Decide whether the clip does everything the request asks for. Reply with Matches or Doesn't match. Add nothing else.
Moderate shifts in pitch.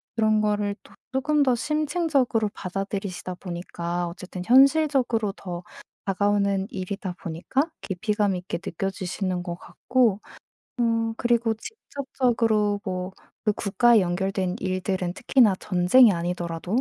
Matches